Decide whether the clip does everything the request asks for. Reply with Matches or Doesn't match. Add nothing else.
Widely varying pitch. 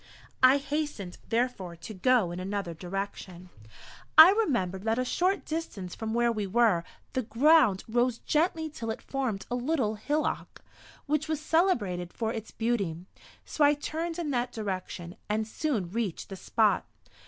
Matches